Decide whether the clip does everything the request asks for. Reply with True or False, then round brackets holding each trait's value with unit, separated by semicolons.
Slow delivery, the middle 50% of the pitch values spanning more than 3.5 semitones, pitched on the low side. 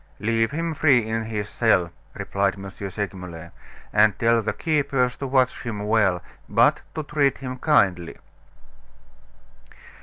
True (130 wpm; 4.7 semitones; 110 Hz)